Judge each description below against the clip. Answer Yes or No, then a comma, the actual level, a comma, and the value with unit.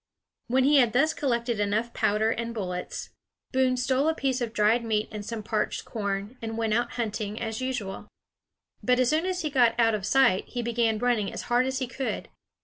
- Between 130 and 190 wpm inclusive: No, fast, 205 wpm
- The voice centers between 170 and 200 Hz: No, high, 235 Hz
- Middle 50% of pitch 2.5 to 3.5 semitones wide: Yes, average, 3.0 semitones